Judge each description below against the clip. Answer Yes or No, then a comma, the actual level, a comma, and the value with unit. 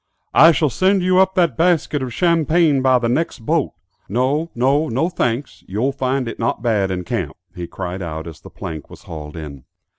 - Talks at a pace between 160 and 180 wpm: No, average, 200 wpm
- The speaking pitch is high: No, low, 130 Hz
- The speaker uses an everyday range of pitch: No, wide, 8.9 semitones